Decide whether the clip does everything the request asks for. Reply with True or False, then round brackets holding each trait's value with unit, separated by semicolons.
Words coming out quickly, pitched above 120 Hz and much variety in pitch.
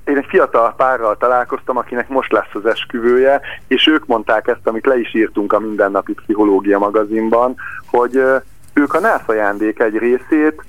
True (165 wpm; 130 Hz; 5.9 semitones)